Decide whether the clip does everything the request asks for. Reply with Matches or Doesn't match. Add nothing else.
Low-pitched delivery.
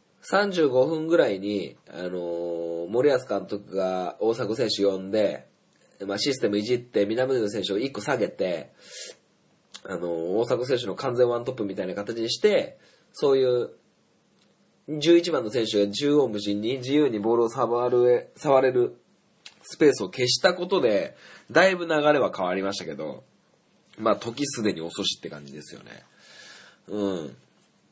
Matches